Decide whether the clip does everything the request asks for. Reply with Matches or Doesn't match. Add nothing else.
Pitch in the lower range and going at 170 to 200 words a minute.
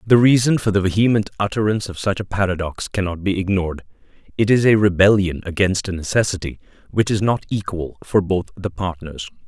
Matches